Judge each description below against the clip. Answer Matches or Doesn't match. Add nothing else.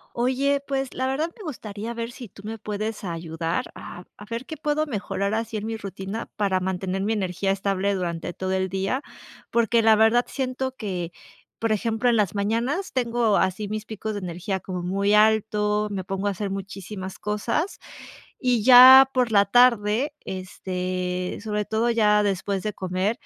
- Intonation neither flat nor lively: Matches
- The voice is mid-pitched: Doesn't match